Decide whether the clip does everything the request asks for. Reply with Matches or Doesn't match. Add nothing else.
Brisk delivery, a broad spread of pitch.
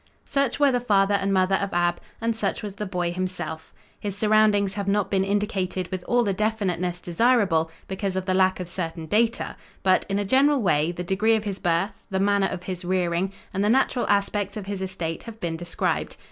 Doesn't match